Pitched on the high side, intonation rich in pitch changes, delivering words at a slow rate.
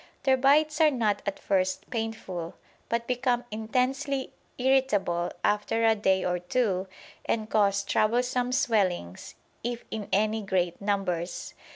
No: high, 220 Hz; average, 4.6 semitones; slow, 130 wpm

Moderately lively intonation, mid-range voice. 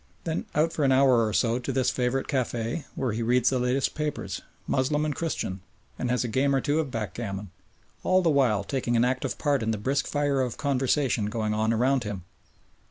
No: average, 3.6 semitones; low, 130 Hz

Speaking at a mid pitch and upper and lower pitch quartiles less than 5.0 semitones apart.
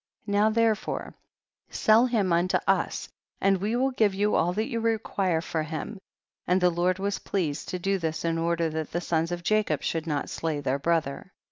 Yes: medium, 180 Hz; average, 4.2 semitones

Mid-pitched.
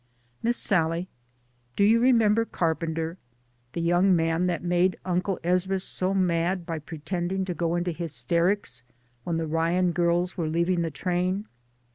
Yes: medium, 175 Hz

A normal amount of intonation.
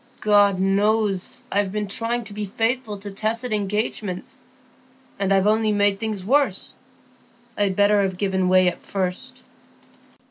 No: narrow, 1.9 semitones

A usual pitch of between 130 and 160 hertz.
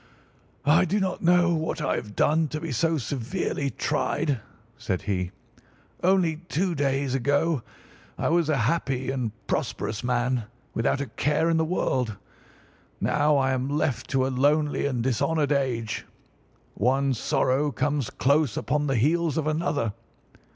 Yes: medium, 140 Hz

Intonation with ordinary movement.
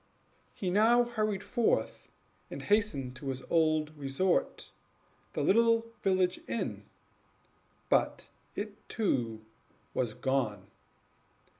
No: wide, 8.1 semitones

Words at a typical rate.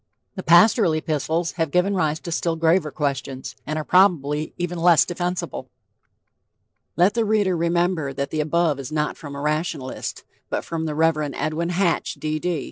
Yes: average, 165 wpm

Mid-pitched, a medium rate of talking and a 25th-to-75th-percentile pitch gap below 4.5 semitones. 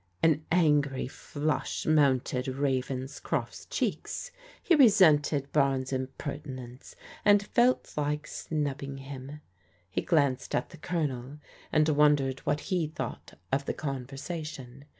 No: medium, 145 Hz; slow, 110 wpm; average, 2.7 semitones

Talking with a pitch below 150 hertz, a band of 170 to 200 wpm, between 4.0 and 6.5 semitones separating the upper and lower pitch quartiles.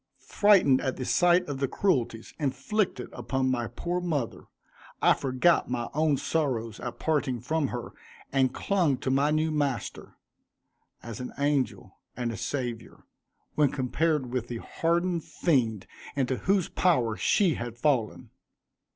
No: low, 135 Hz; average, 140 wpm; average, 4.7 semitones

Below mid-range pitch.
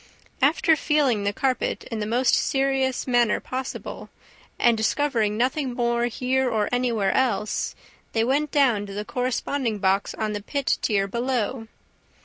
No: high, 240 Hz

